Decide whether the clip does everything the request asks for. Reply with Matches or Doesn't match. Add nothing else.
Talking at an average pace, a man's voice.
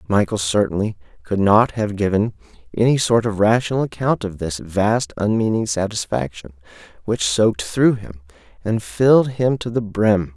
Matches